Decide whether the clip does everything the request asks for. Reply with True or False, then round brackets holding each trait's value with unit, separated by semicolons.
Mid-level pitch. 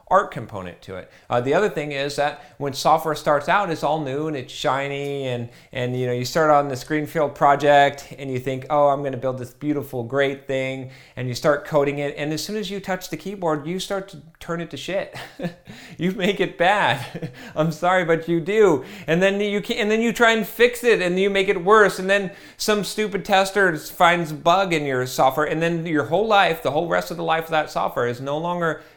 True (155 Hz)